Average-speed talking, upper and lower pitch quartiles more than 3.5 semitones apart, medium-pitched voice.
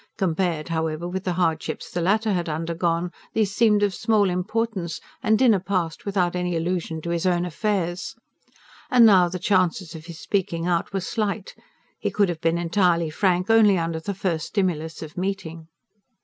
No: average, 175 wpm; average, 3.0 semitones; medium, 180 Hz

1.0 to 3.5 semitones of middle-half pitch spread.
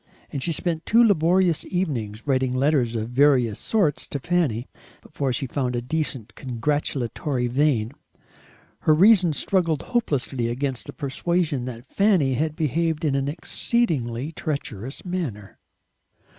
No: average, 4.9 semitones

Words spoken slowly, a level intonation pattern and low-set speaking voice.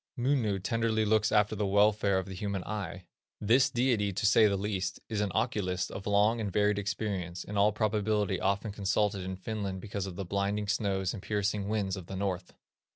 No: average, 195 wpm; narrow, 1.8 semitones; low, 100 Hz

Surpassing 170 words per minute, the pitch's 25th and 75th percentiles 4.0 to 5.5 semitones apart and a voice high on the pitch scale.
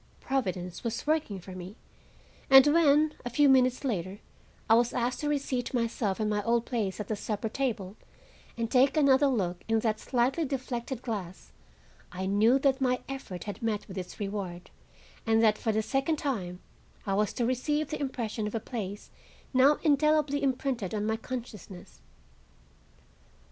No: average, 165 wpm; average, 4.7 semitones; high, 235 Hz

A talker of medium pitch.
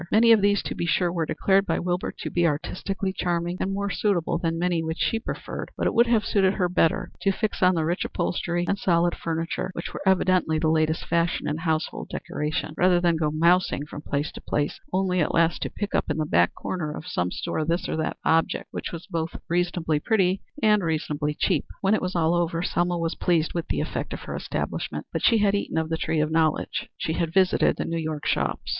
Yes: medium, 170 Hz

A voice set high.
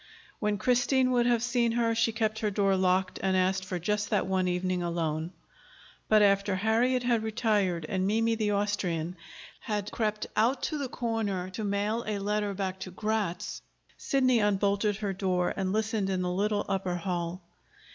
Yes: high, 205 Hz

